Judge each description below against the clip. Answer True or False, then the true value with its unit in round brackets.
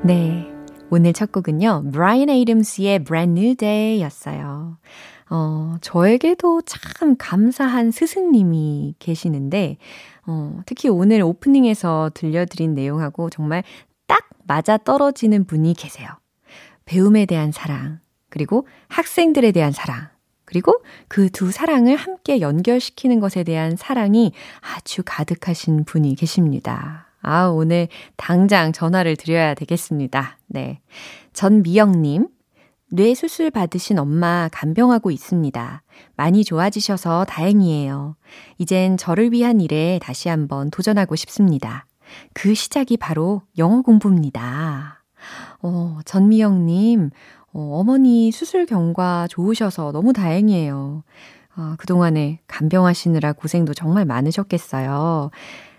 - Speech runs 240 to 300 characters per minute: True (275 characters per minute)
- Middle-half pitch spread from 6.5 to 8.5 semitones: False (5.2 semitones)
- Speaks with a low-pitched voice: False (175 Hz)